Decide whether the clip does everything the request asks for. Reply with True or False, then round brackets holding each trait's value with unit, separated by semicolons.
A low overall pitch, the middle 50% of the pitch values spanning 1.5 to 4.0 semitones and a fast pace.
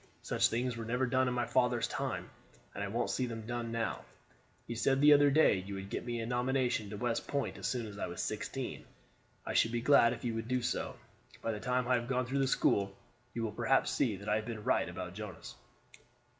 True (120 Hz; 2.7 semitones; 240 wpm)